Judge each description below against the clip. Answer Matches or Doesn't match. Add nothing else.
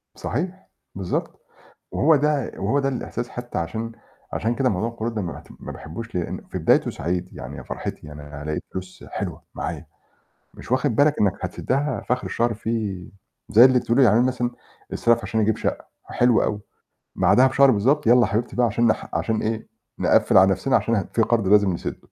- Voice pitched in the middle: Doesn't match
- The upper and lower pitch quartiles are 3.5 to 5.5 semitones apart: Matches